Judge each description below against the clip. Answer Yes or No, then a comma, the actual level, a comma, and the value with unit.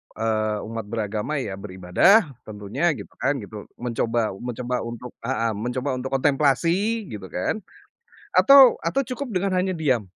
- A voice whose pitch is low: Yes, low, 125 Hz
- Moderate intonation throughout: No, wide, 7.5 semitones